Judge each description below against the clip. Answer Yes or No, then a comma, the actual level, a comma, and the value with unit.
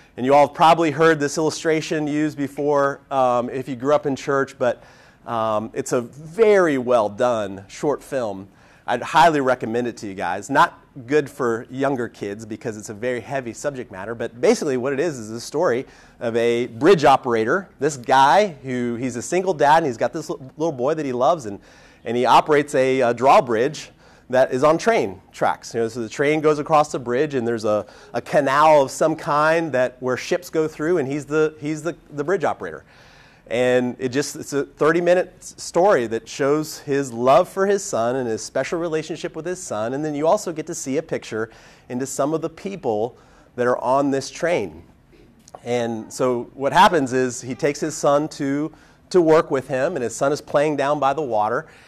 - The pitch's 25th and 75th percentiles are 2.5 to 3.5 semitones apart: No, average, 4.2 semitones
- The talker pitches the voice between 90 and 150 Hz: Yes, medium, 140 Hz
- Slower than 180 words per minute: No, fast, 205 wpm